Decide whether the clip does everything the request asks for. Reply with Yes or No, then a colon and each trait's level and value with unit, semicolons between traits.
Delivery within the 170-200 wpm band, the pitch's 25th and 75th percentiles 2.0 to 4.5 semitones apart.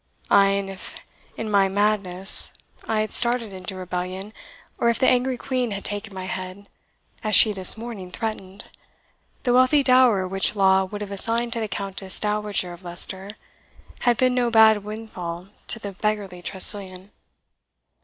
No: average, 160 wpm; average, 2.9 semitones